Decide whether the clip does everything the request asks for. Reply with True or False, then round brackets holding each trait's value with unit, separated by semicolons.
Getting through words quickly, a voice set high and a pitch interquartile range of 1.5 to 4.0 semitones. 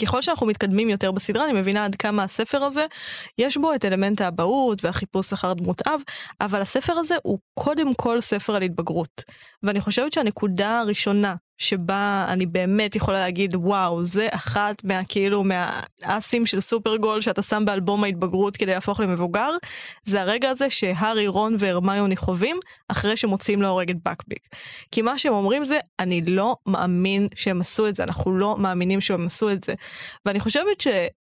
True (160 wpm; 205 Hz; 2.8 semitones)